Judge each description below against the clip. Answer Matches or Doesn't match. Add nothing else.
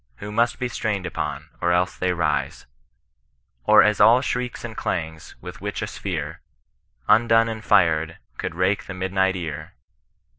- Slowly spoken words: Doesn't match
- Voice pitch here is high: Doesn't match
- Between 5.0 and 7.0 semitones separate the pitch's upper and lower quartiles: Matches